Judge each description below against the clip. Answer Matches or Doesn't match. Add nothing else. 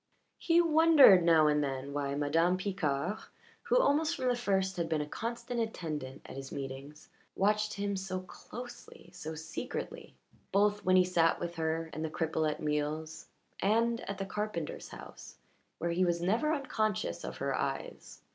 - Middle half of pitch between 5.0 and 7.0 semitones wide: Matches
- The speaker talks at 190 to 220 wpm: Doesn't match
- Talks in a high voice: Doesn't match